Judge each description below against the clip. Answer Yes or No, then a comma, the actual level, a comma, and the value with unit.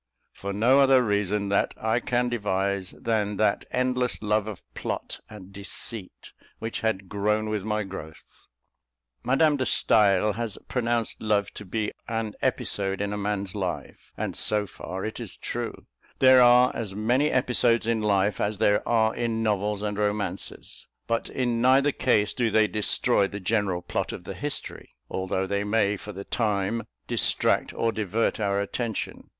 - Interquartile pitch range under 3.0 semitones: Yes, narrow, 2.5 semitones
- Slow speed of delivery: No, average, 165 wpm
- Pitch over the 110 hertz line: No, low, 105 Hz